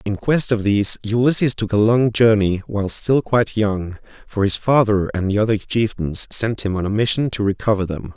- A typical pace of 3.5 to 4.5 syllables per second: No, 5.2 syllables/s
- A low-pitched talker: Yes, low, 105 Hz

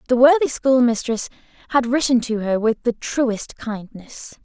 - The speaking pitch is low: No, high, 240 Hz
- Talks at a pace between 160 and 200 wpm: No, average, 150 wpm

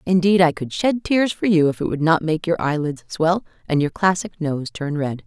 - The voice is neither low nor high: Yes, medium, 170 Hz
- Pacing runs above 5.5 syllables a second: No, 5.0 syllables/s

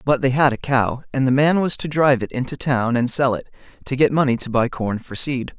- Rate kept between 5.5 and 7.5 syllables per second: Yes, 5.6 syllables/s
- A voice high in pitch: No, low, 130 Hz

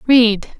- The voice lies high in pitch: Yes, high, 230 Hz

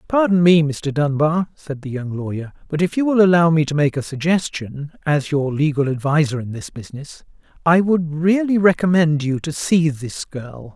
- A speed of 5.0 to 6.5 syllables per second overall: No, 4.8 syllables/s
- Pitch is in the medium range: Yes, medium, 155 Hz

